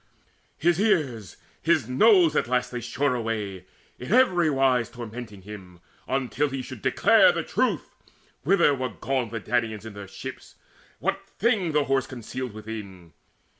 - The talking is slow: No, average, 155 wpm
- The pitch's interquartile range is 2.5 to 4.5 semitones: No, average, 5.1 semitones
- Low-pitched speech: Yes, low, 125 Hz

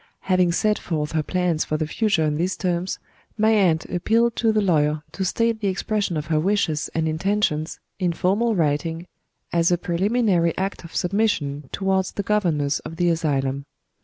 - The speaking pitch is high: No, medium, 175 Hz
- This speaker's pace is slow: No, average, 175 wpm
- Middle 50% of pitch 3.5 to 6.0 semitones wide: Yes, average, 4.3 semitones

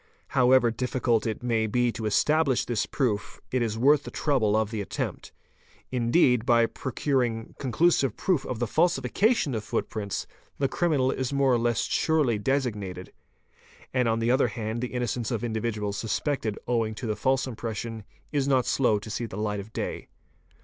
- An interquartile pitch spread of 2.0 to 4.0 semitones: Yes, average, 3.2 semitones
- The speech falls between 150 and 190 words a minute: Yes, average, 175 wpm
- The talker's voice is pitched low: Yes, low, 120 Hz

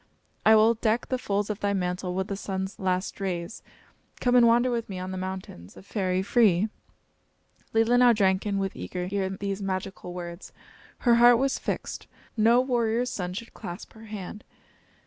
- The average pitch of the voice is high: Yes, high, 200 Hz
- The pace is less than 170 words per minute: No, average, 175 wpm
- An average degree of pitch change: Yes, average, 3.6 semitones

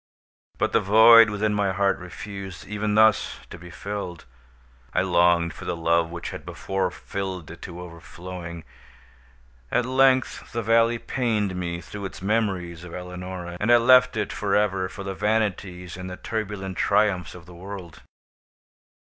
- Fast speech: No, average, 160 wpm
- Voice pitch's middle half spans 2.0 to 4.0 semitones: Yes, average, 3.1 semitones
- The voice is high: No, very low, 95 Hz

